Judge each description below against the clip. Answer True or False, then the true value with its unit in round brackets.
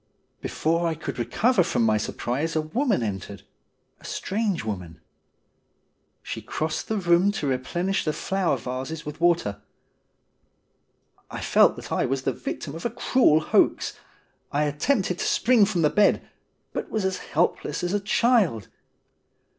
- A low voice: False (165 Hz)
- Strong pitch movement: True (6.5 semitones)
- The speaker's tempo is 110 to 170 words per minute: True (155 wpm)